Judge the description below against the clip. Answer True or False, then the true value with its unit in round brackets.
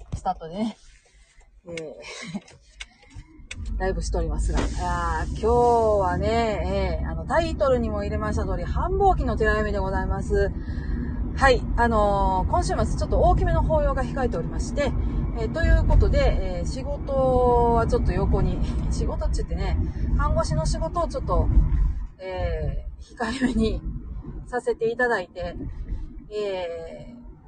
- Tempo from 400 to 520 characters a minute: False (280 characters per minute)